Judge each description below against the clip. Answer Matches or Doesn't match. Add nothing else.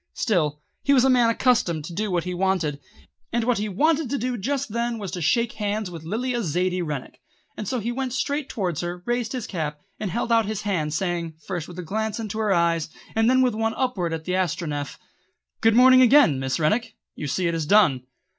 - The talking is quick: Matches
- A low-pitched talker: Doesn't match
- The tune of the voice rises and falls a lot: Matches